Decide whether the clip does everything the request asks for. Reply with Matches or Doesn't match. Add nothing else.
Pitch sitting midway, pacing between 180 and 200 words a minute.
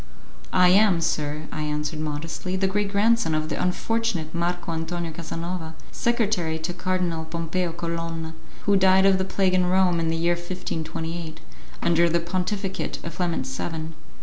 Doesn't match